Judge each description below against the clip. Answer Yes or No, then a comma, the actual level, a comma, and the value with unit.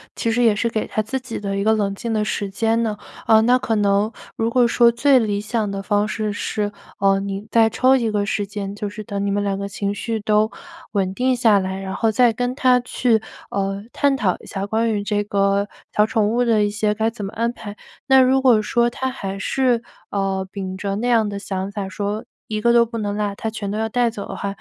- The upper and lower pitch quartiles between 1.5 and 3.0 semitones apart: Yes, narrow, 2.5 semitones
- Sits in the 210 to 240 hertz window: Yes, high, 215 Hz